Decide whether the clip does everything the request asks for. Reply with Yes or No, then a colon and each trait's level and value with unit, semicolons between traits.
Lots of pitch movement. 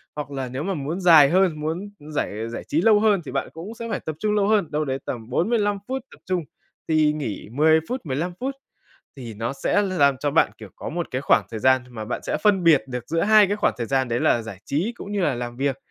Yes: wide, 6.9 semitones